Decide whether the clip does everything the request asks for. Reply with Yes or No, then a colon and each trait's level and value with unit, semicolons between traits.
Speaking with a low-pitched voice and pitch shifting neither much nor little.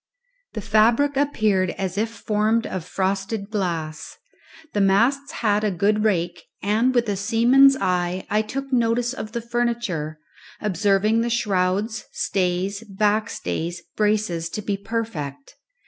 No: high, 210 Hz; average, 3.6 semitones